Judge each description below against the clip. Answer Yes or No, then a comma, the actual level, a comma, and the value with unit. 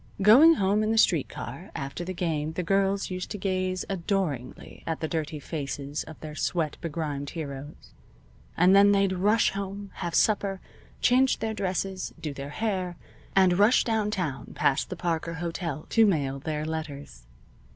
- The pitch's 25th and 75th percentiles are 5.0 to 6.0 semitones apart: No, average, 4.5 semitones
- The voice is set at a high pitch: No, medium, 175 Hz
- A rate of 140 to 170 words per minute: Yes, average, 160 wpm